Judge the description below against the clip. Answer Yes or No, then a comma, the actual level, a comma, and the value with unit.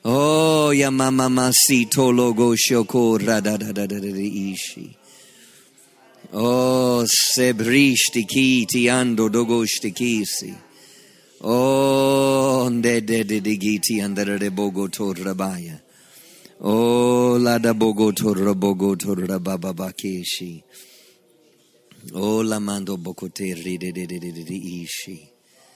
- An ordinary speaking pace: No, slow, 70 wpm